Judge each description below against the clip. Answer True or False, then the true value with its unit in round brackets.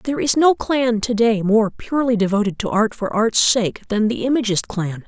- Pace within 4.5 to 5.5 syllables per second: True (5.0 syllables/s)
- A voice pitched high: True (225 Hz)